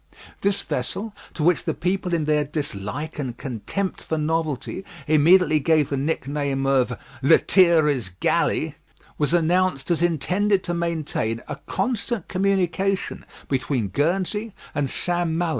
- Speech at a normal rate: No, slow, 130 wpm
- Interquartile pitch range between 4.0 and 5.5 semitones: Yes, average, 4.4 semitones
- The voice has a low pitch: No, medium, 160 Hz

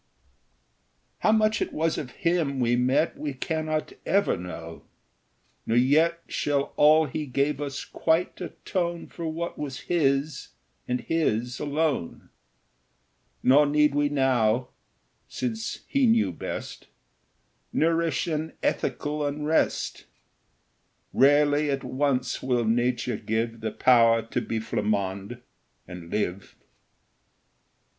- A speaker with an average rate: No, slow, 115 wpm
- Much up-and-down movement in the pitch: No, average, 4.6 semitones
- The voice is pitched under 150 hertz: Yes, medium, 140 Hz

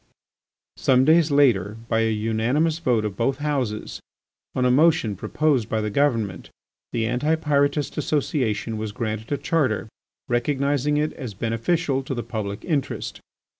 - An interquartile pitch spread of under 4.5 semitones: No, average, 4.9 semitones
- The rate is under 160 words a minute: Yes, average, 150 wpm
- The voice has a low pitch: Yes, low, 125 Hz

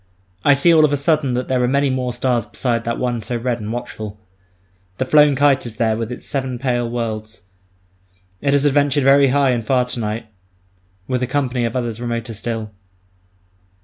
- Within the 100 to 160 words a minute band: No, average, 195 wpm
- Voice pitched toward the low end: Yes, low, 125 Hz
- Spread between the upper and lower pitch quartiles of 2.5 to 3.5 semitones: Yes, average, 2.9 semitones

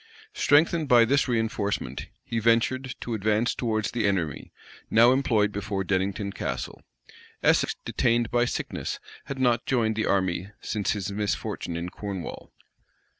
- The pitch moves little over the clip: No, average, 3.3 semitones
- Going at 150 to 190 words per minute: No, slow, 135 wpm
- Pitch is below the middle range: Yes, low, 110 Hz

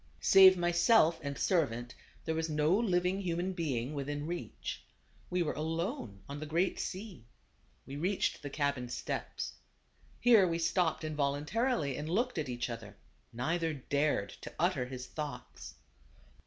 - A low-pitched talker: No, medium, 155 Hz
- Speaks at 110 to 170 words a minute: Yes, average, 145 wpm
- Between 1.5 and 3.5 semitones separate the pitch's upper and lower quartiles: No, average, 4.1 semitones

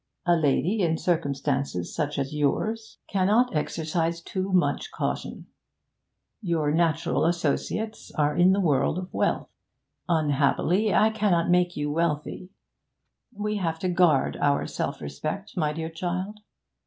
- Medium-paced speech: No, slow, 130 wpm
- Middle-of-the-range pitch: Yes, medium, 170 Hz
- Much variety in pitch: No, average, 3.8 semitones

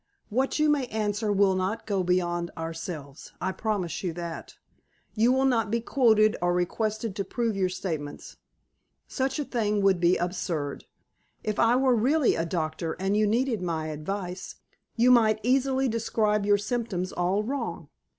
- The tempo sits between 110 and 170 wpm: Yes, average, 160 wpm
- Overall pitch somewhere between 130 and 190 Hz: No, high, 205 Hz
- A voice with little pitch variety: No, average, 4.7 semitones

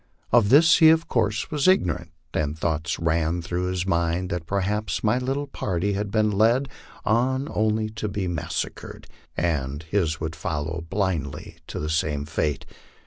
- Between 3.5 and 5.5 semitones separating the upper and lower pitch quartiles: Yes, average, 5.1 semitones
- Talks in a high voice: No, very low, 90 Hz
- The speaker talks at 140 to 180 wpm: Yes, average, 160 wpm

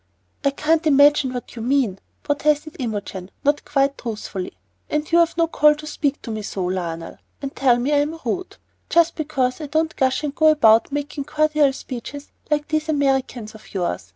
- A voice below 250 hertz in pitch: No, very high, 280 Hz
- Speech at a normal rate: Yes, average, 180 wpm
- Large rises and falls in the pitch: No, average, 4.3 semitones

